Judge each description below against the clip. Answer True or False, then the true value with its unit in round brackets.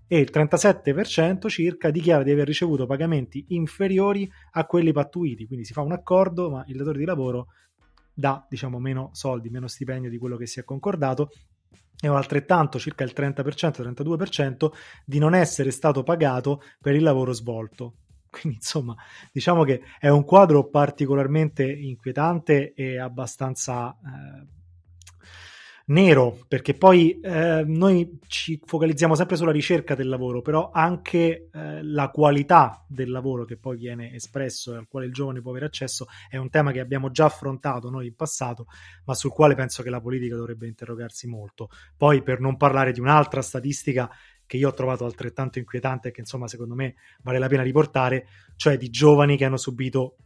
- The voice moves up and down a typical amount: True (3.5 semitones)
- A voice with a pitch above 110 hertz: True (135 Hz)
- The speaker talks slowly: False (170 wpm)